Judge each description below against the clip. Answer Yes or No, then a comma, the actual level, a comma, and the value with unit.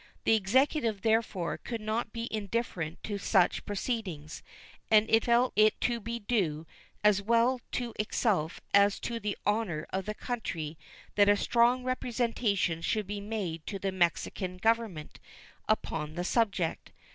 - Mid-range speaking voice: No, high, 210 Hz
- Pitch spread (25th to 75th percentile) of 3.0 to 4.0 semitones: Yes, average, 3.7 semitones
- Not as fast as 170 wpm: Yes, average, 145 wpm